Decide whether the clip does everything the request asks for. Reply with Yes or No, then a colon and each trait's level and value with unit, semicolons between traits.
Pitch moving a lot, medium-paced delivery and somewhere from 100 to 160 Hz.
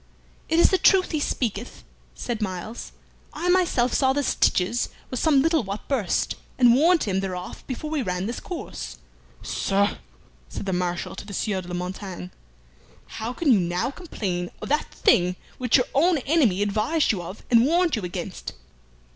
No: wide, 7.6 semitones; average, 175 wpm; high, 230 Hz